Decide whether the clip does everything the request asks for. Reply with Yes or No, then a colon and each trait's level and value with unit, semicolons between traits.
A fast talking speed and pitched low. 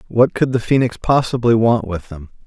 No: average, 195 wpm; low, 115 Hz